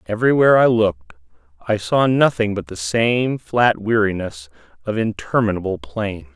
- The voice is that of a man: Yes, male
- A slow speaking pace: Yes, slow, 130 wpm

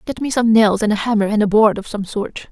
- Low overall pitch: No, high, 215 Hz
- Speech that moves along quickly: Yes, fast, 310 wpm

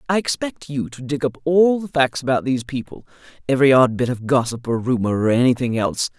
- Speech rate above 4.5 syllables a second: Yes, 6.0 syllables/s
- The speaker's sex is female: Yes, female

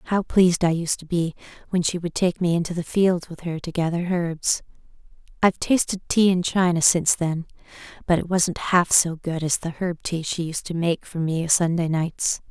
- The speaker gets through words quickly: Yes, fast, 215 wpm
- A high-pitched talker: No, medium, 170 Hz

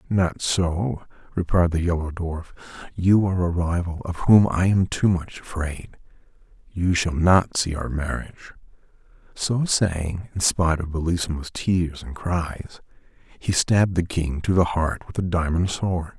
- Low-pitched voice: Yes, very low, 85 Hz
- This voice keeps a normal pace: Yes, average, 160 wpm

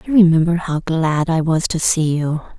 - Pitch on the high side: No, medium, 165 Hz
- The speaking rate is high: Yes, fast, 230 wpm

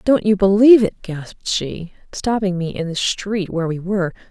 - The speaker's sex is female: Yes, female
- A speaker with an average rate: Yes, average, 195 wpm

